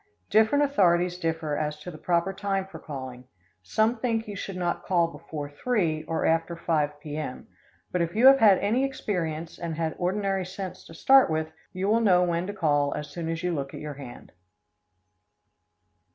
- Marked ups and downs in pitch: No, average, 4.2 semitones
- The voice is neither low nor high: Yes, medium, 170 Hz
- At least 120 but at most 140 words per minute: No, average, 185 wpm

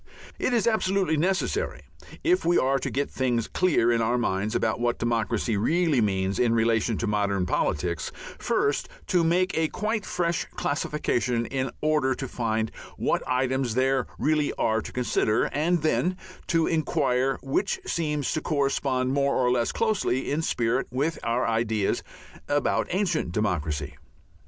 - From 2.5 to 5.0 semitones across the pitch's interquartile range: No, wide, 5.6 semitones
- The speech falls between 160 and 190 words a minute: No, average, 150 wpm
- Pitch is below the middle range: Yes, low, 130 Hz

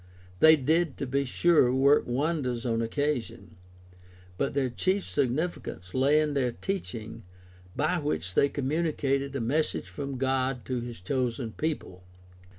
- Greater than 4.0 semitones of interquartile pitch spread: No, average, 3.7 semitones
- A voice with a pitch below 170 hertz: Yes, low, 135 Hz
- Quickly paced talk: No, average, 140 wpm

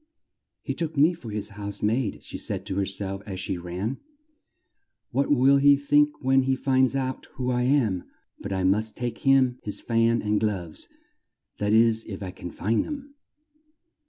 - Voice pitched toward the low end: Yes, low, 115 Hz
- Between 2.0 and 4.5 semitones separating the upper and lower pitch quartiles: No, average, 5.0 semitones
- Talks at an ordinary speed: Yes, average, 180 wpm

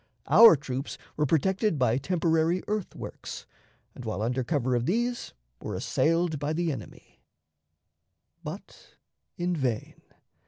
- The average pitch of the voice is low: No, medium, 155 Hz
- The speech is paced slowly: Yes, slow, 120 wpm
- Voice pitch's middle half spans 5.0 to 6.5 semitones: Yes, average, 5.3 semitones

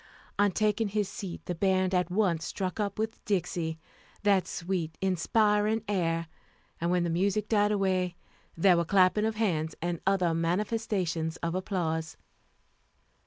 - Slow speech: No, average, 145 wpm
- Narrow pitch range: No, average, 3.3 semitones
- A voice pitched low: No, medium, 185 Hz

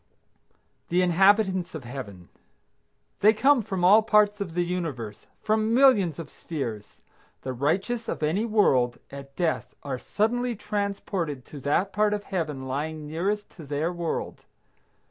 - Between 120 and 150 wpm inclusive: Yes, average, 145 wpm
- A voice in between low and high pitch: Yes, medium, 175 Hz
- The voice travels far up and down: Yes, wide, 6.3 semitones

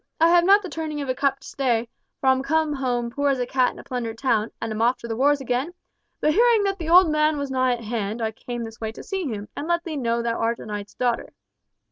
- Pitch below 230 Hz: No, very high, 260 Hz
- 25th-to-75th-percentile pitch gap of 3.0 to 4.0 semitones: No, average, 4.9 semitones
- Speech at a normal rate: No, fast, 275 wpm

